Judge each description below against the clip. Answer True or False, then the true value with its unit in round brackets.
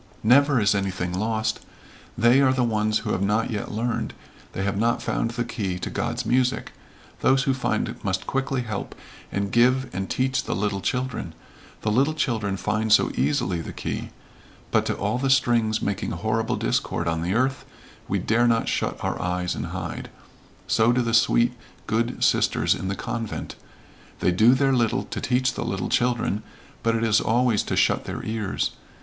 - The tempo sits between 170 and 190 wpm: True (180 wpm)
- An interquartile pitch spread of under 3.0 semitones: False (3.7 semitones)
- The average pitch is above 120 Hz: False (115 Hz)